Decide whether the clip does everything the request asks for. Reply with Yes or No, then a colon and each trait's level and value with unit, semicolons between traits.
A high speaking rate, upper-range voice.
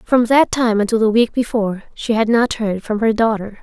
Yes: fast, 230 wpm; high, 225 Hz